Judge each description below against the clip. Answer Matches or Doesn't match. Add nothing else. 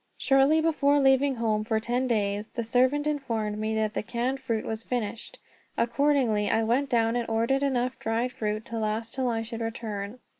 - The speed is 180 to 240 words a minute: Matches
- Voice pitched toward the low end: Doesn't match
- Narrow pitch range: Doesn't match